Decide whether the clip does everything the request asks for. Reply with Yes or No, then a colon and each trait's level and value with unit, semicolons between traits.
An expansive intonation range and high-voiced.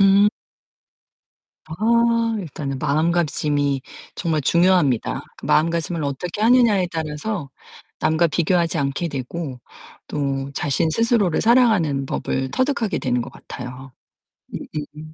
No: wide, 5.7 semitones; medium, 160 Hz